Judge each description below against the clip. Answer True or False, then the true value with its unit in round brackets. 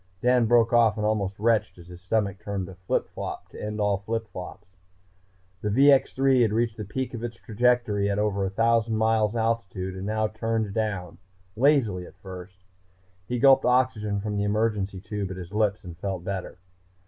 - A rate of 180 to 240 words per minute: True (185 wpm)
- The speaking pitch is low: True (105 Hz)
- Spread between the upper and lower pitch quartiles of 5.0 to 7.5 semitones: False (2.7 semitones)